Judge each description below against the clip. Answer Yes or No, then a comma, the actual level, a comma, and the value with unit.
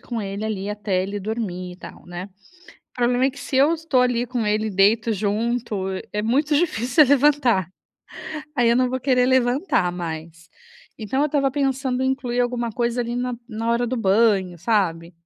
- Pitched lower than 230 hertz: No, high, 235 Hz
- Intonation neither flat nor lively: Yes, average, 4.2 semitones